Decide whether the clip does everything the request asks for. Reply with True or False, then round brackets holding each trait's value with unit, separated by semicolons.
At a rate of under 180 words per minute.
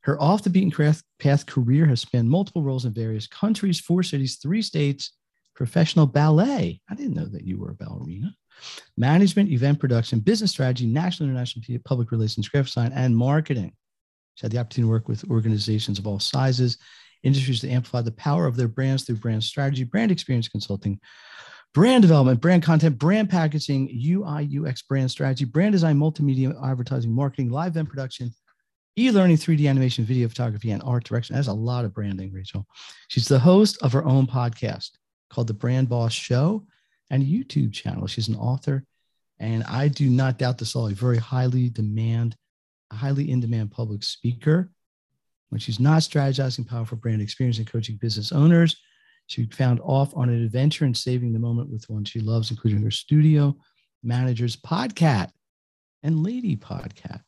True (170 wpm)